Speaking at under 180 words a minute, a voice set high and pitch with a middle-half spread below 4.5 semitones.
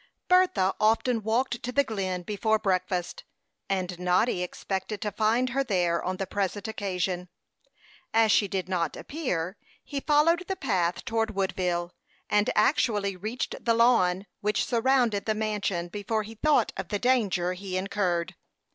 Yes: average, 150 wpm; high, 205 Hz; average, 3.9 semitones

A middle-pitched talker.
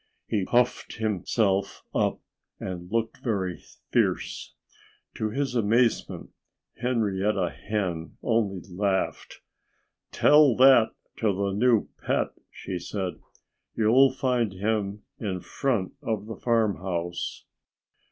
No: low, 105 Hz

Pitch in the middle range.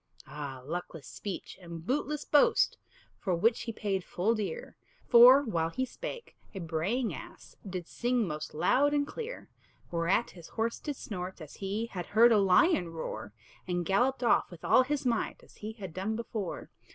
No: high, 205 Hz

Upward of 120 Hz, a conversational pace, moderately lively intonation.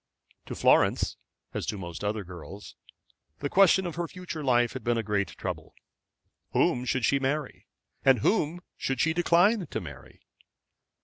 No: low, 135 Hz; average, 160 wpm; wide, 8.2 semitones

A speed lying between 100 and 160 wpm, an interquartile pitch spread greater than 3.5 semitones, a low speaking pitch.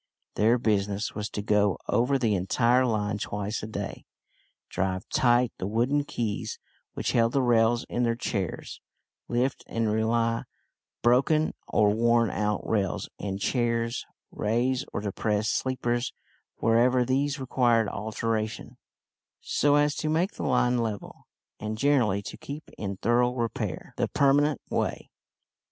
No: average, 140 wpm; average, 2.9 semitones; low, 115 Hz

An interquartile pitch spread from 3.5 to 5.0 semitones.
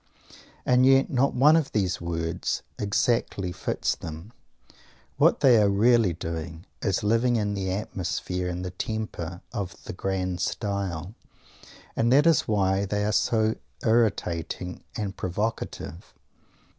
Yes: average, 4.2 semitones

